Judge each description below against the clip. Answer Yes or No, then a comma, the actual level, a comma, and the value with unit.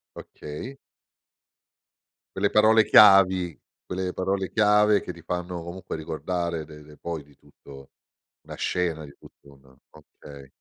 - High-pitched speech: No, very low, 85 Hz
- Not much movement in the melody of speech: No, average, 4.1 semitones